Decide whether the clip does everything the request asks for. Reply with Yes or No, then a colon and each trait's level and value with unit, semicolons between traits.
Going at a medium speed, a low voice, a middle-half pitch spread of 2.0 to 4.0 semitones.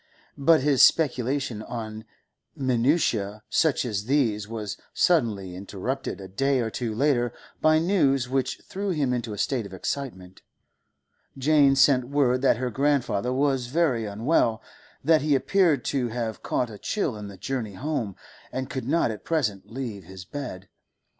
No: average, 155 wpm; low, 125 Hz; average, 4.6 semitones